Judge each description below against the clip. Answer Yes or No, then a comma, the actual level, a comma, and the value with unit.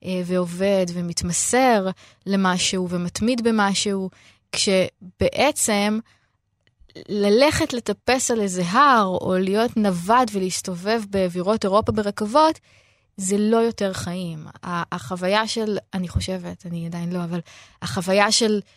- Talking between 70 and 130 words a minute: Yes, slow, 100 wpm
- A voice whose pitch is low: No, high, 195 Hz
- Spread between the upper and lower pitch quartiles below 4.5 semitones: Yes, average, 3.3 semitones